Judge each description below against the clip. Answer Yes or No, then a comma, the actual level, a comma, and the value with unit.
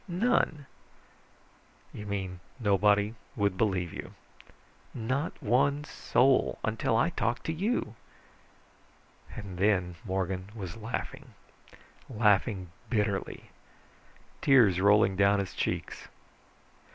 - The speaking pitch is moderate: No, low, 105 Hz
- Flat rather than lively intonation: No, average, 4.3 semitones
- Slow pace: Yes, slow, 95 wpm